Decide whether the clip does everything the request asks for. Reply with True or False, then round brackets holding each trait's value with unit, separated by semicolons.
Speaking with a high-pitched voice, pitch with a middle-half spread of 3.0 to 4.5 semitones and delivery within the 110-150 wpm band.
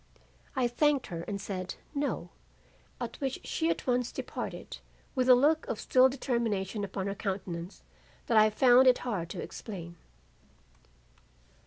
False (235 Hz; 5.0 semitones; 145 wpm)